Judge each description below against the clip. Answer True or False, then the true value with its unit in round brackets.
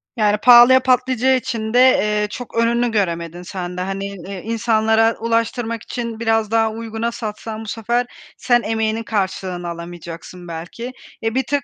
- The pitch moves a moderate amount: True (3.1 semitones)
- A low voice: False (225 Hz)